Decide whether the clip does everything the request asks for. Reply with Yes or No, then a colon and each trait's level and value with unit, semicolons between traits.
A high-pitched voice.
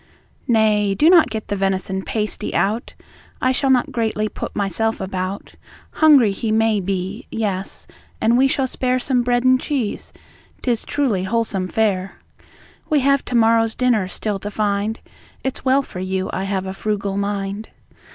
Yes: high, 215 Hz